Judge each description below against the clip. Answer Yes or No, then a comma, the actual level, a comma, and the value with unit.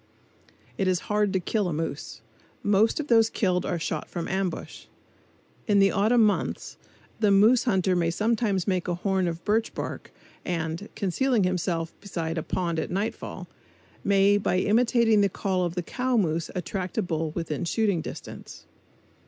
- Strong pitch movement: No, average, 3.5 semitones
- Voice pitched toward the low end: No, high, 190 Hz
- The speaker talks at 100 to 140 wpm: No, average, 165 wpm